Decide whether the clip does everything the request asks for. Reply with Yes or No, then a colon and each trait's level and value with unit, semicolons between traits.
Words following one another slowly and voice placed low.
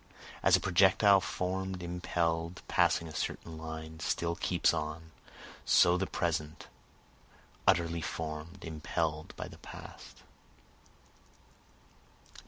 Yes: slow, 100 wpm; very low, 85 Hz